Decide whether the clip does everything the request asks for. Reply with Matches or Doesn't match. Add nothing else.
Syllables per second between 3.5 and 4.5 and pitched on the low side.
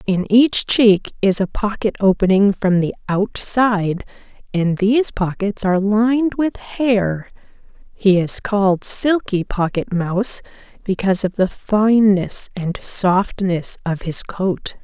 Doesn't match